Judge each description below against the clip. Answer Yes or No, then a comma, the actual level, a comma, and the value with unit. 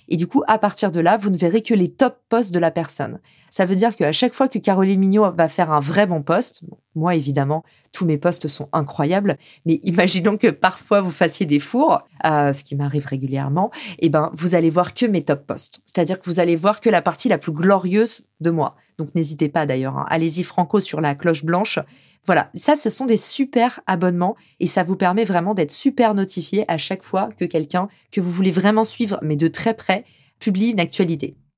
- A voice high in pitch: No, medium, 180 Hz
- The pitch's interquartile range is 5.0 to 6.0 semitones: No, average, 4.4 semitones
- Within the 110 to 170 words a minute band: No, fast, 220 wpm